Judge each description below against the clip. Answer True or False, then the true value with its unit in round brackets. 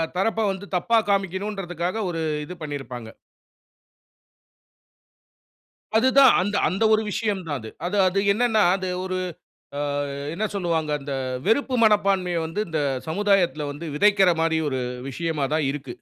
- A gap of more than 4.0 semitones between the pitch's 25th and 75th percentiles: True (4.4 semitones)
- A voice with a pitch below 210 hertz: True (185 Hz)